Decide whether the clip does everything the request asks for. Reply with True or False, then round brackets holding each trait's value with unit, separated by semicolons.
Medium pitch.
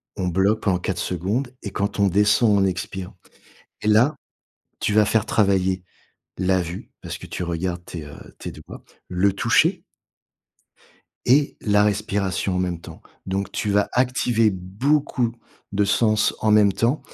False (100 Hz)